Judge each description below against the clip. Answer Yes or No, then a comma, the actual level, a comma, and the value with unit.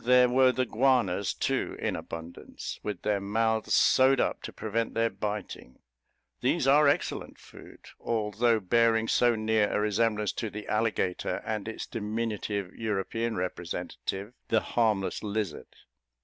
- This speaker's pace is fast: No, slow, 135 wpm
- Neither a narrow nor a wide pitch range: No, narrow, 2.1 semitones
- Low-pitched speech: Yes, low, 110 Hz